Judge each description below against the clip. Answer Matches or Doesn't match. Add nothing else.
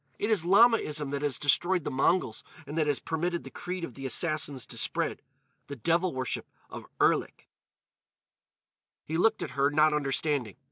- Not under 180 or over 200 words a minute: Doesn't match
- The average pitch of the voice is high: Doesn't match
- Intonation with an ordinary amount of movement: Matches